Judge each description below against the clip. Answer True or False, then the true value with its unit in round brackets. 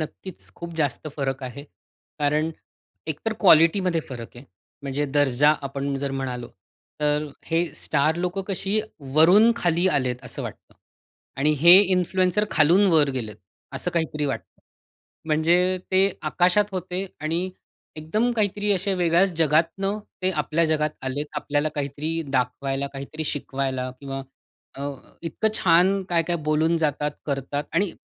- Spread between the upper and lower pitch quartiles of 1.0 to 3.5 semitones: False (4.4 semitones)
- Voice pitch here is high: False (155 Hz)